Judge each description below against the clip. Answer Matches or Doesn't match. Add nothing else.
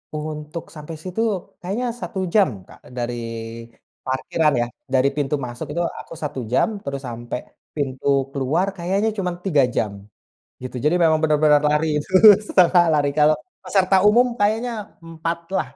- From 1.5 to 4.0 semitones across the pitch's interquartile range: Doesn't match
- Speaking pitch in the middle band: Matches